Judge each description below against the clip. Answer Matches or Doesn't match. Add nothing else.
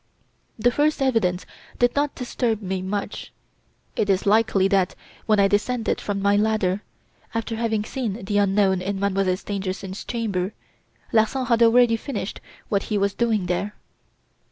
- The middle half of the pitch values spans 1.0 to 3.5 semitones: Matches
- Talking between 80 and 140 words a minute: Doesn't match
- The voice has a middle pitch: Doesn't match